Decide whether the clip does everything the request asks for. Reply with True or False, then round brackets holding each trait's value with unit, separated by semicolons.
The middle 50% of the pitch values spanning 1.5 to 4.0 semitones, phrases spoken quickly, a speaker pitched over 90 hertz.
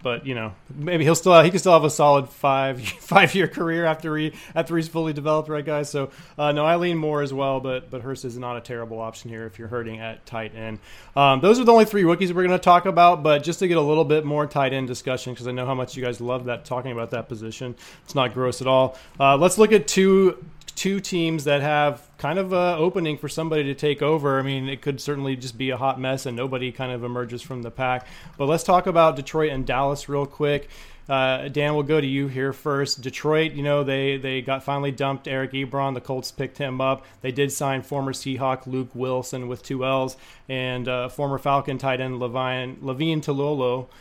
True (3.2 semitones; 240 wpm; 140 Hz)